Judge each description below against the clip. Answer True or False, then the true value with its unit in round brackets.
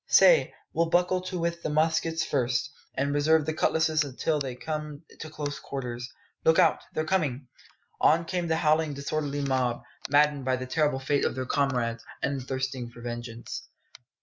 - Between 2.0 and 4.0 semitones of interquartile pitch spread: True (3.5 semitones)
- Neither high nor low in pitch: True (145 Hz)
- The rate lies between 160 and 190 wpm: True (170 wpm)